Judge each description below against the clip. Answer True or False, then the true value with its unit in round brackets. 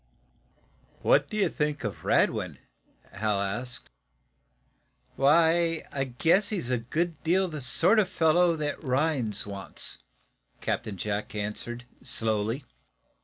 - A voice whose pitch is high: False (135 Hz)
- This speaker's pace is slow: True (120 wpm)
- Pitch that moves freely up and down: True (7.2 semitones)